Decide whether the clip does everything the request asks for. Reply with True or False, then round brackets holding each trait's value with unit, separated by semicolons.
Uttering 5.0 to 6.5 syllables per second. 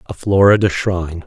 True (5.6 syllables/s)